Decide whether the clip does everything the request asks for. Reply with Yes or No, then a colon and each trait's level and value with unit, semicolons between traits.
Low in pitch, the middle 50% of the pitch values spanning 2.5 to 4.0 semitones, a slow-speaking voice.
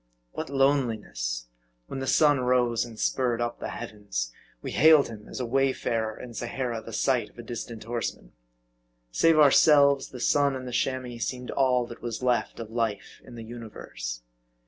No: low, 120 Hz; average, 2.8 semitones; average, 180 wpm